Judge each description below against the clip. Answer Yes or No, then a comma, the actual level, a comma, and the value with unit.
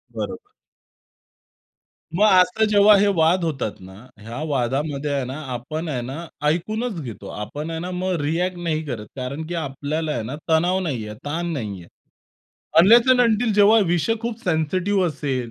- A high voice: No, medium, 160 Hz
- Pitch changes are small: No, average, 5.3 semitones